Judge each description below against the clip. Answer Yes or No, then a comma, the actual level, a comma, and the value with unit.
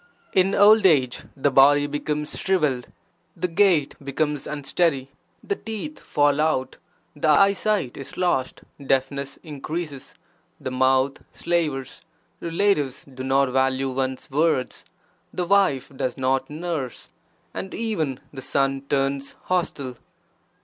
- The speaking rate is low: Yes, slow, 120 wpm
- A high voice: No, medium, 145 Hz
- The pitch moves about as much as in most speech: Yes, average, 4.3 semitones